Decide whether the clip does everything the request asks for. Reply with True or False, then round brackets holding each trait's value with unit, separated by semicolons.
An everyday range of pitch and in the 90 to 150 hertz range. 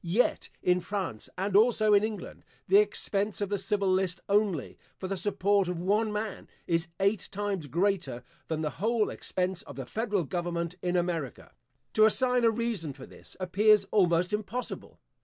False (3.2 semitones; 195 Hz)